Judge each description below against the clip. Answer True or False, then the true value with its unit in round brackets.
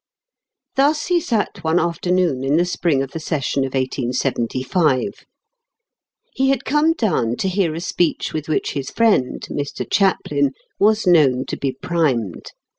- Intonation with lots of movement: True (6.5 semitones)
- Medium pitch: True (160 Hz)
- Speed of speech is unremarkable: True (150 wpm)